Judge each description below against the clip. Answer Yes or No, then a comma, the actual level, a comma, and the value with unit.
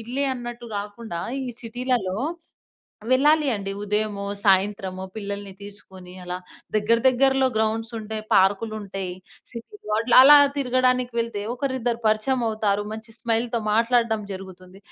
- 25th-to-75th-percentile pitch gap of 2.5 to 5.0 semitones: Yes, average, 3.3 semitones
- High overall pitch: Yes, high, 220 Hz